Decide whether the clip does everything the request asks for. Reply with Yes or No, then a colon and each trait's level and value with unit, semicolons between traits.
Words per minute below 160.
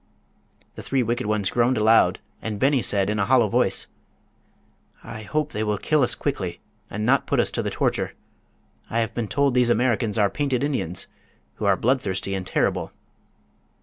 No: average, 180 wpm